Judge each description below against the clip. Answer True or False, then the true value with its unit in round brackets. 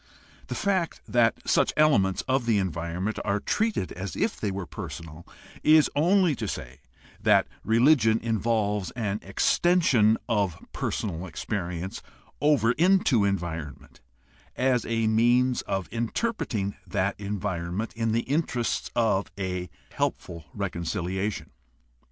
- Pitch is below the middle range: True (105 Hz)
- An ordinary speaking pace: False (120 wpm)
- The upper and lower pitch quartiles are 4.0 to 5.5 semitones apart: True (4.7 semitones)